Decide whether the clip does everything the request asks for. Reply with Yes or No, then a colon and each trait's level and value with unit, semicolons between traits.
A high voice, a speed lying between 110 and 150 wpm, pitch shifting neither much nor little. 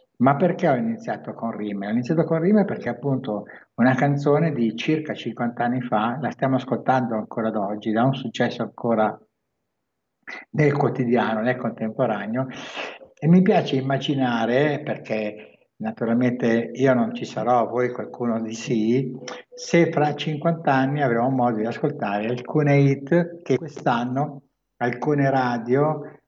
No: low, 130 Hz; average, 140 wpm; average, 4.1 semitones